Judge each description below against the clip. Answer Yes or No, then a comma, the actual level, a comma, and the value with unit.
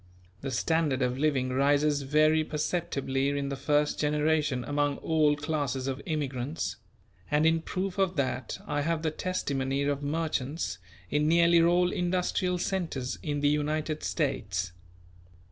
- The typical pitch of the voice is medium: Yes, medium, 150 Hz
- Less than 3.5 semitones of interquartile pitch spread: Yes, average, 2.8 semitones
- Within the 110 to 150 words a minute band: Yes, average, 140 wpm